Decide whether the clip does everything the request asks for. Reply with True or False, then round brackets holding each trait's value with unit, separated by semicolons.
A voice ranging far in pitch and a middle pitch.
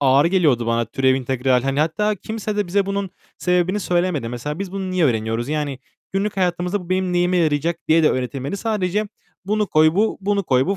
True (6.3 semitones; 175 Hz)